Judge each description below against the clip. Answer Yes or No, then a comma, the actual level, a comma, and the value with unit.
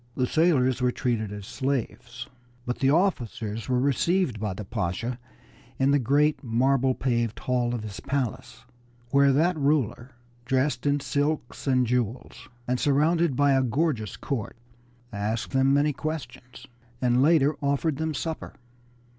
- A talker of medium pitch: No, low, 130 Hz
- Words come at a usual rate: Yes, average, 145 wpm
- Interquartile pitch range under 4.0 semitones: Yes, average, 3.2 semitones